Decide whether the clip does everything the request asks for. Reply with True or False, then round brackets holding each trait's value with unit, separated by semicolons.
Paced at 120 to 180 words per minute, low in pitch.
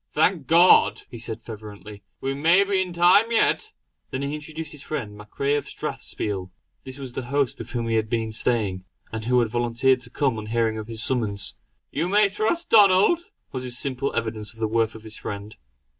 False (205 wpm; 125 Hz)